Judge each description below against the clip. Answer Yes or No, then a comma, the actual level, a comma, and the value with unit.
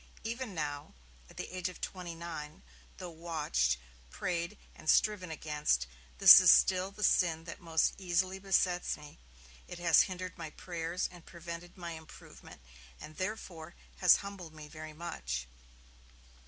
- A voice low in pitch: No, medium, 170 Hz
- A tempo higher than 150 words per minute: No, average, 145 wpm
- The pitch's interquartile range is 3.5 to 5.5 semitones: No, average, 2.7 semitones